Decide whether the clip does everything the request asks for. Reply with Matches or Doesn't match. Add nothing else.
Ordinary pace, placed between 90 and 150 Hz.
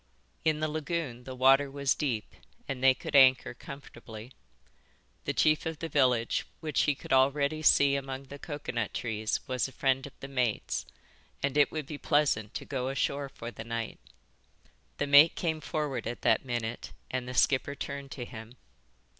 Matches